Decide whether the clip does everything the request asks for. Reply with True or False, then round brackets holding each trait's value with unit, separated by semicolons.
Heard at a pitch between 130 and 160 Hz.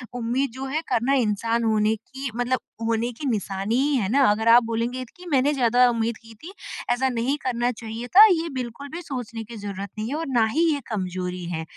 False (235 Hz)